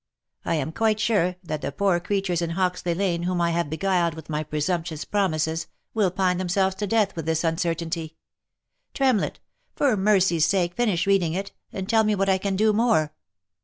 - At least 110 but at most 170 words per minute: No, average, 185 wpm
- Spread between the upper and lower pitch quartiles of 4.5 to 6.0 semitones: No, average, 3.1 semitones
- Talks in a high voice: No, medium, 180 Hz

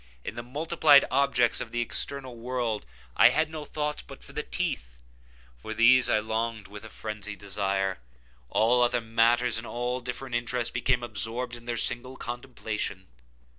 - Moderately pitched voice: No, low, 120 Hz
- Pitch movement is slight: Yes, narrow, 2.3 semitones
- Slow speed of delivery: No, average, 165 wpm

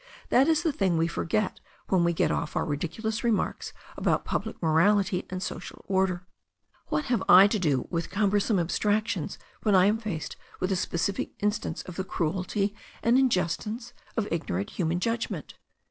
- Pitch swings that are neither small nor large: Yes, average, 3.9 semitones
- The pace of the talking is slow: No, average, 165 wpm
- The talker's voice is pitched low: No, high, 190 Hz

